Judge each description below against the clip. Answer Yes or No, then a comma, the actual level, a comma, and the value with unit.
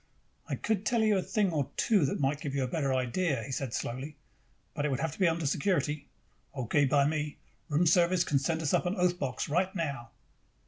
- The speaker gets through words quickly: Yes, fast, 225 wpm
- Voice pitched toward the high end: No, medium, 150 Hz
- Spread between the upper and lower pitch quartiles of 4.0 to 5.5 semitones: Yes, average, 4.5 semitones